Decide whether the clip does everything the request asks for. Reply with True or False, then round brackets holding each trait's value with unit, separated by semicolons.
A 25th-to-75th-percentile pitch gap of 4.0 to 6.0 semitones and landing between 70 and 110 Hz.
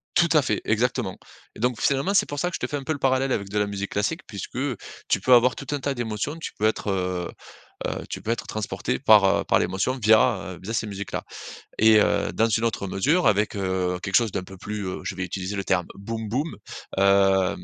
True (4.5 semitones; 105 Hz)